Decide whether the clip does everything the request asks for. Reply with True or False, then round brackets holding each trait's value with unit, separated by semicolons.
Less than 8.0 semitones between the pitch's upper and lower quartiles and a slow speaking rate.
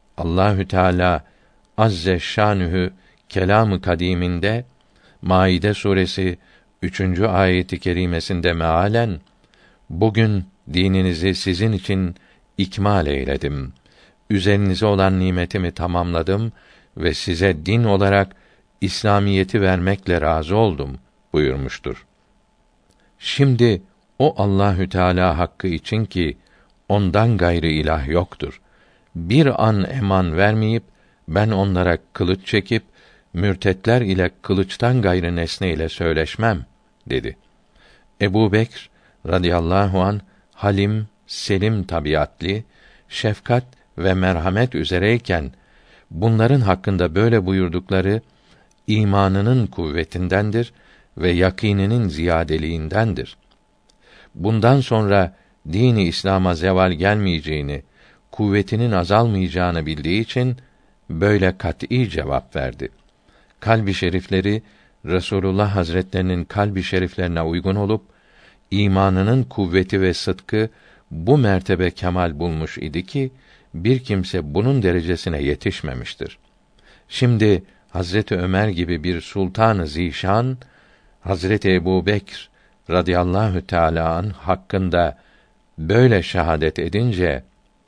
True (2.9 semitones; 90 wpm)